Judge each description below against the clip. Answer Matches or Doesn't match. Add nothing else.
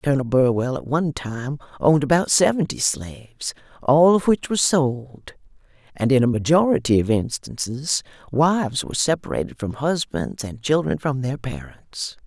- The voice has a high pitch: Doesn't match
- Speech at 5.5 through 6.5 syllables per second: Doesn't match